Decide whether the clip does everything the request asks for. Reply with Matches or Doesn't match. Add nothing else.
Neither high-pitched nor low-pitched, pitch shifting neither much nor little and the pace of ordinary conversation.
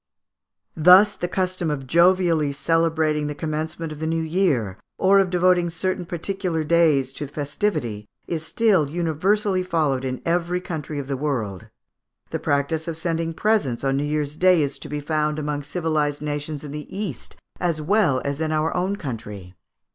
Matches